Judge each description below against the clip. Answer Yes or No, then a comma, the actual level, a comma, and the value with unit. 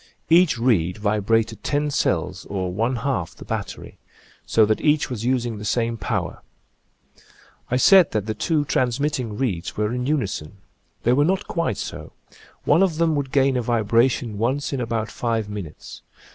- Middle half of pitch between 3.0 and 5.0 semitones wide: Yes, average, 4.7 semitones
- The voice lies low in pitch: Yes, low, 120 Hz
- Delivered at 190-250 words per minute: No, average, 165 wpm